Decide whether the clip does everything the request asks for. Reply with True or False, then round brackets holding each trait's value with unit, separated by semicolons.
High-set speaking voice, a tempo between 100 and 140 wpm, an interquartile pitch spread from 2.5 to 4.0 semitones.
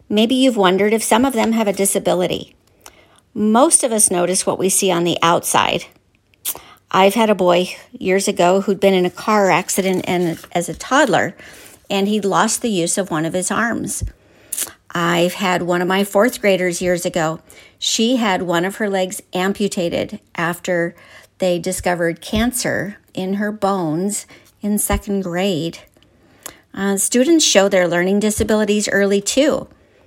False (195 Hz; 160 wpm; 2.9 semitones)